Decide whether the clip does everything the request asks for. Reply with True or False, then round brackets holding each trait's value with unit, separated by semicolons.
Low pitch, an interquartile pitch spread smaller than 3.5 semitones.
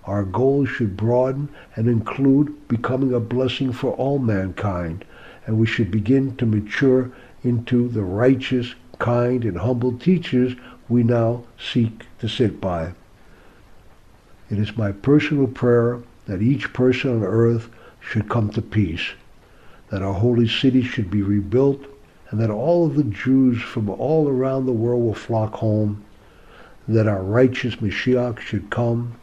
True (120 Hz; 3.1 semitones)